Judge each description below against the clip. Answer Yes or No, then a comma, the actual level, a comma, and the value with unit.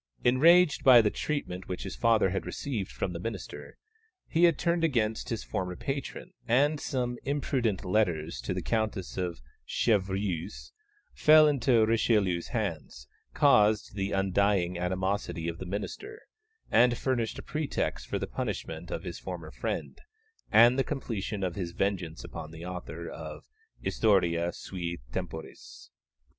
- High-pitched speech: No, low, 105 Hz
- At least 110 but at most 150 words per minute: Yes, average, 145 wpm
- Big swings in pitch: Yes, wide, 5.9 semitones